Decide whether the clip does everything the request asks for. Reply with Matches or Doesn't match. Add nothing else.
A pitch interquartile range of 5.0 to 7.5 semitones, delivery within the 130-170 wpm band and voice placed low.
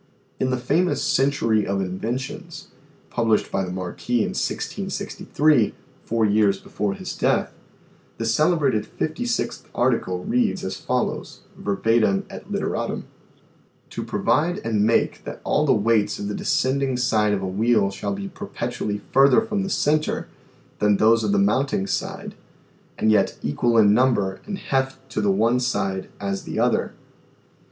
Matches